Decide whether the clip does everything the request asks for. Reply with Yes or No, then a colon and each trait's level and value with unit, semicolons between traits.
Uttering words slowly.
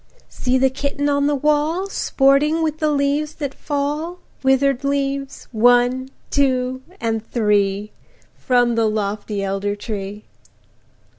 Yes: slow, 105 wpm